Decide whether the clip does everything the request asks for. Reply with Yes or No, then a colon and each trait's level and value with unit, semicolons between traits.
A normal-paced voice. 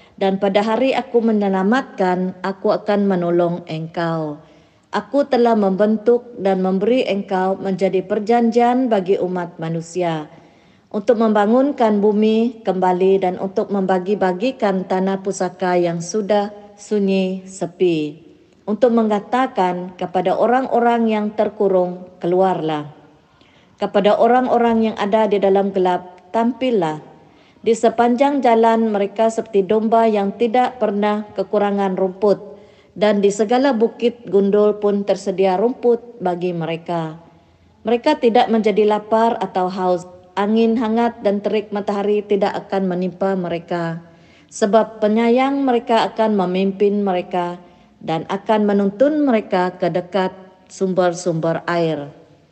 Yes: average, 110 wpm